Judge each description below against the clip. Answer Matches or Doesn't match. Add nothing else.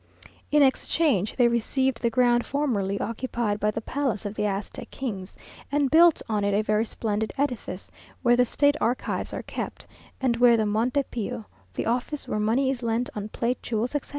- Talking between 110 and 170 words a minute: Doesn't match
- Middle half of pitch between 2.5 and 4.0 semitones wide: Matches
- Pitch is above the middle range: Matches